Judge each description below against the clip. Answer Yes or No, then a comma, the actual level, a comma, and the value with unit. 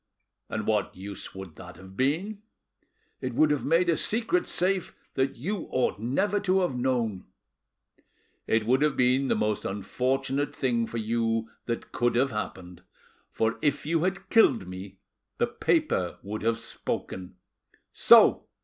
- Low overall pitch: Yes, low, 125 Hz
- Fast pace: No, average, 150 wpm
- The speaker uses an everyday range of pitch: No, wide, 6.2 semitones